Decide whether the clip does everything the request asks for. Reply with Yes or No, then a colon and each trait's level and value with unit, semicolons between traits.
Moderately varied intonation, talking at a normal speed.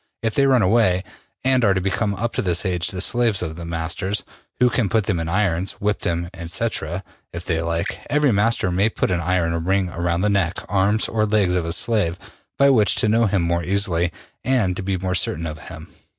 No: average, 3.9 semitones; fast, 220 wpm